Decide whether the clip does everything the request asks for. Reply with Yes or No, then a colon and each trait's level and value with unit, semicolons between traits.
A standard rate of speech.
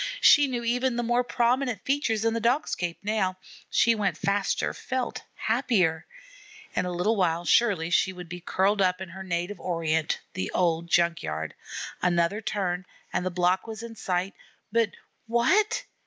Yes: average, 170 wpm